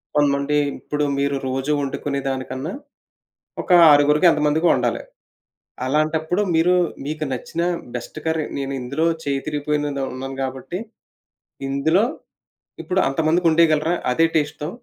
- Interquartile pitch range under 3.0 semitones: Yes, narrow, 2.5 semitones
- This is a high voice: No, medium, 150 Hz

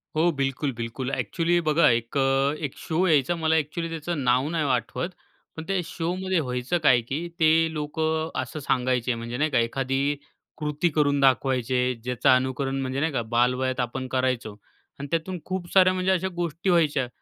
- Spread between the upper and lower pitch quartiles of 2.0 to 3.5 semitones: No, average, 4.3 semitones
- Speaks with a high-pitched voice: No, medium, 140 Hz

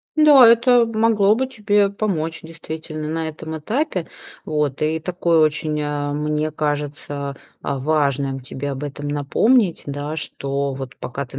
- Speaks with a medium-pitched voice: Yes, medium, 155 Hz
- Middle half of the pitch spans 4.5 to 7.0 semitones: Yes, wide, 5.5 semitones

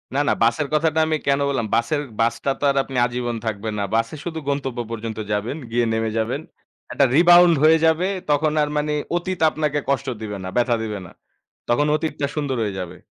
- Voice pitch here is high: No, low, 135 Hz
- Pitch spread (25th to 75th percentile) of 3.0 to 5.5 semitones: Yes, average, 5.1 semitones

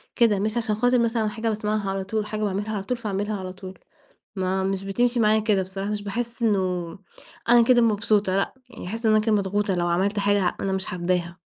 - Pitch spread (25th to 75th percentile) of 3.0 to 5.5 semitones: No, narrow, 2.4 semitones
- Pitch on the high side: Yes, high, 205 Hz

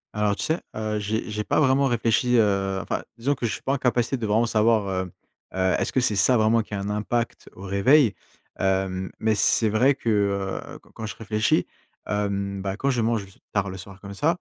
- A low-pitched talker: Yes, low, 105 Hz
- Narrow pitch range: No, average, 3.0 semitones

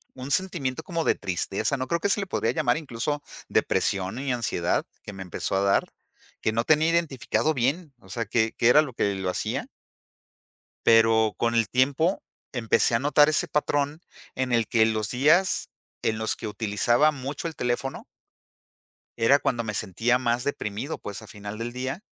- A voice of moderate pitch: No, low, 125 Hz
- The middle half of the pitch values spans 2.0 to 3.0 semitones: No, average, 4.8 semitones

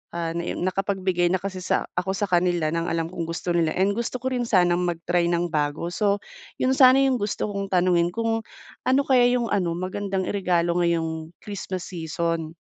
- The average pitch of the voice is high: No, medium, 180 Hz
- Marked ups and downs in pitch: No, average, 3.0 semitones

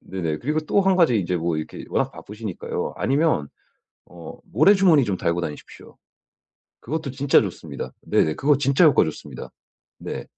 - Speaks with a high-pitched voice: No, low, 130 Hz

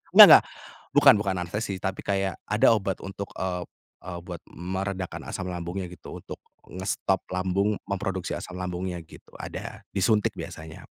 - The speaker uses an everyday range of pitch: No, narrow, 1.5 semitones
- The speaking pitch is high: No, very low, 95 Hz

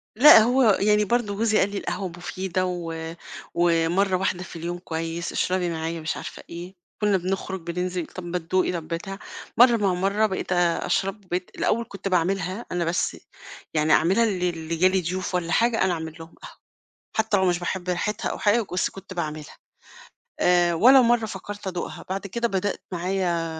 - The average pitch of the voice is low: No, medium, 185 Hz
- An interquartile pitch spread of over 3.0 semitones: No, average, 2.7 semitones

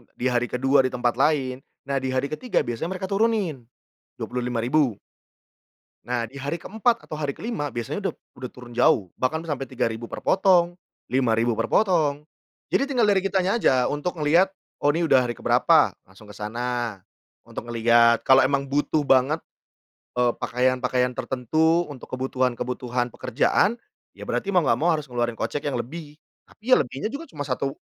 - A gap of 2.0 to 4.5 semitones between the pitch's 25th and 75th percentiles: No, average, 4.9 semitones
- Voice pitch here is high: No, low, 135 Hz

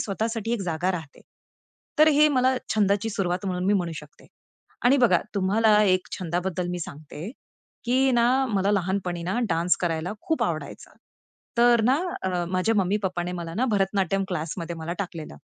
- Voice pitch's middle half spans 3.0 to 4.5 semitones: Yes, average, 4.0 semitones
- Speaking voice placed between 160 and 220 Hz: Yes, high, 190 Hz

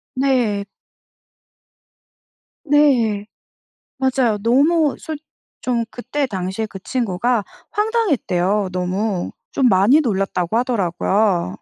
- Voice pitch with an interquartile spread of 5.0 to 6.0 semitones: Yes, wide, 5.5 semitones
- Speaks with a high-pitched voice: Yes, high, 230 Hz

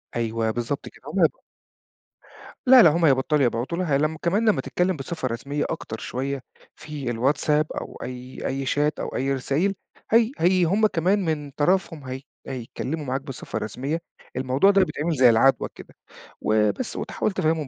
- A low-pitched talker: No, medium, 145 Hz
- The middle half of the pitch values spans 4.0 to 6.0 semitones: Yes, average, 4.7 semitones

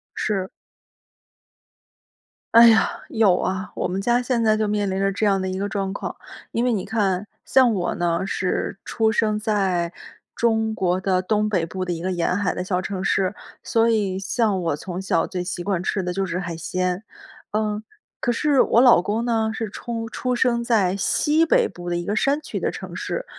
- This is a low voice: No, high, 200 Hz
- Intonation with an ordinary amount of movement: Yes, average, 3.4 semitones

